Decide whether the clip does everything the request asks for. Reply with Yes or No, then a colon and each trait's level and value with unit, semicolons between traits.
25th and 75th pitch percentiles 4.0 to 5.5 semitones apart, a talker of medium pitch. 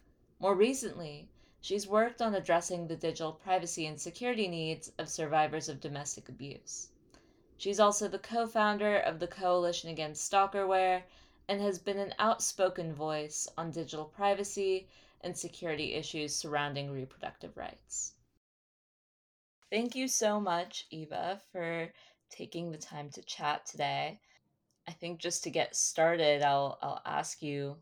Yes: average, 4.3 semitones; medium, 170 Hz